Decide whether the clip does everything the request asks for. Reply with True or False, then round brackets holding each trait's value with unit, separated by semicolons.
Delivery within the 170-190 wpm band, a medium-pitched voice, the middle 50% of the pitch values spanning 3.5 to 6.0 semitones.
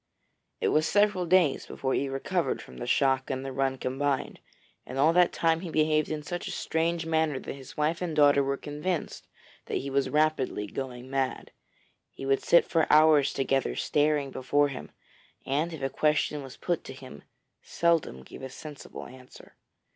False (180 wpm; 145 Hz; 3.0 semitones)